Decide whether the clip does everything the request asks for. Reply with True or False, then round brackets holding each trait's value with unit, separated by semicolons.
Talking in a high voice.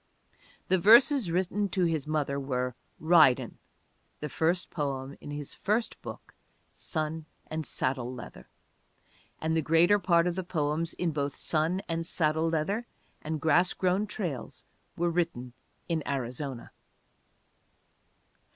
False (160 Hz)